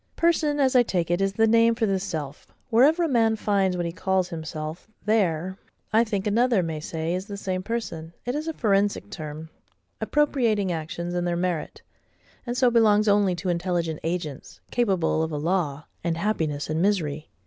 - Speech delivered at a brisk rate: No, average, 185 wpm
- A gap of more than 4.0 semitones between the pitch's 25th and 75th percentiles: Yes, average, 5.2 semitones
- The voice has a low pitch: No, high, 190 Hz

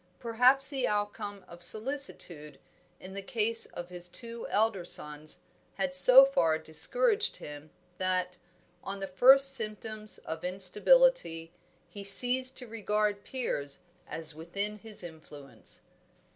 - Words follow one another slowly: Yes, slow, 125 wpm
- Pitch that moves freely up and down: Yes, wide, 6.2 semitones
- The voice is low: No, high, 205 Hz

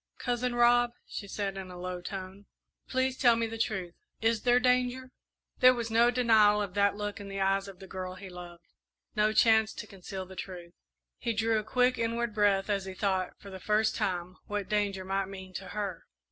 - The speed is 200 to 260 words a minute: Yes, fast, 205 wpm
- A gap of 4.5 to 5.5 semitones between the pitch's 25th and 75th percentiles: No, average, 3.3 semitones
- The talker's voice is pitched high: Yes, high, 205 Hz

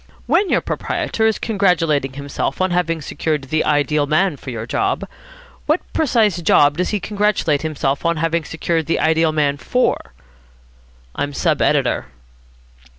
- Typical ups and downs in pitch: Yes, average, 4.4 semitones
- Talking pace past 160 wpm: No, average, 150 wpm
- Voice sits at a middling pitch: Yes, medium, 160 Hz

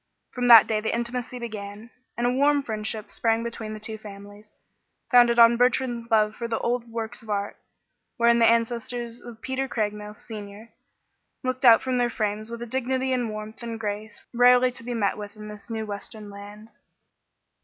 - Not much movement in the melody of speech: Yes, narrow, 2.2 semitones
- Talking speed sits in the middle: Yes, average, 185 wpm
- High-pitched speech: Yes, high, 230 Hz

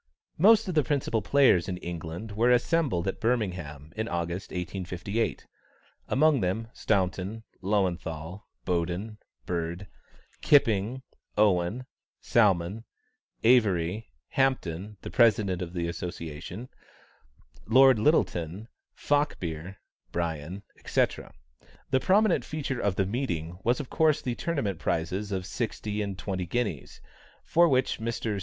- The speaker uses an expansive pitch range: Yes, wide, 5.9 semitones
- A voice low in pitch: Yes, low, 100 Hz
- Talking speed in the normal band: No, slow, 115 wpm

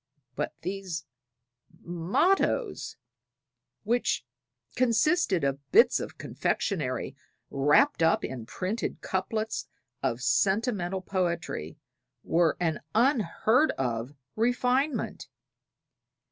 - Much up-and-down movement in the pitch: Yes, wide, 7.1 semitones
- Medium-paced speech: No, slow, 80 wpm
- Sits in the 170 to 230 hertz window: Yes, high, 190 Hz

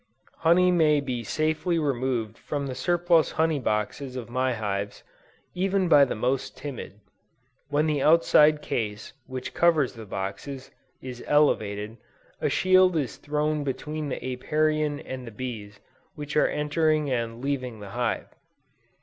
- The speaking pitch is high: No, medium, 140 Hz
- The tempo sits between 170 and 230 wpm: No, average, 140 wpm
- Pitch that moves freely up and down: No, average, 4.4 semitones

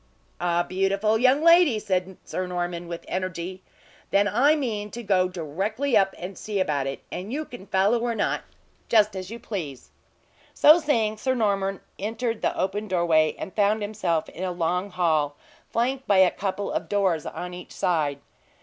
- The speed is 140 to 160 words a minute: No, average, 175 wpm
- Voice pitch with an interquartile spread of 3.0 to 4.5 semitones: Yes, average, 3.7 semitones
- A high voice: Yes, high, 195 Hz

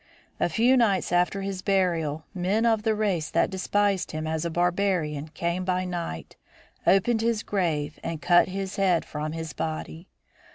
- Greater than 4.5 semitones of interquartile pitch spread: No, average, 3.5 semitones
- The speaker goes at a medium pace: Yes, average, 165 wpm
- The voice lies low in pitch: No, medium, 180 Hz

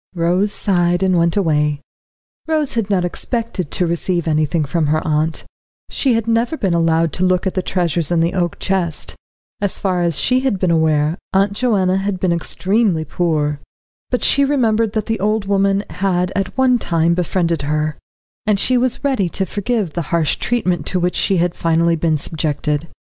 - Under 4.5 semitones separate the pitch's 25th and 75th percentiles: Yes, average, 3.6 semitones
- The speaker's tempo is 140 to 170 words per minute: No, average, 185 wpm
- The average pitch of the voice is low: No, medium, 180 Hz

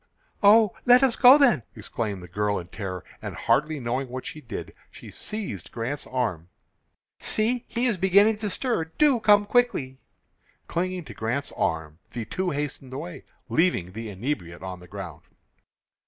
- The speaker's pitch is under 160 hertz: Yes, medium, 140 Hz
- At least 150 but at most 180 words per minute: Yes, average, 160 wpm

